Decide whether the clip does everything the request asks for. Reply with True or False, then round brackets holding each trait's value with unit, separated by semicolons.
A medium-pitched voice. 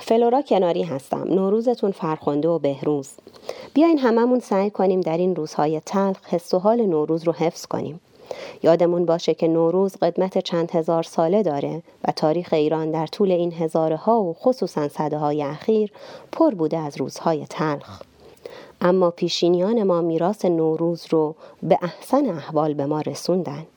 True (175 Hz)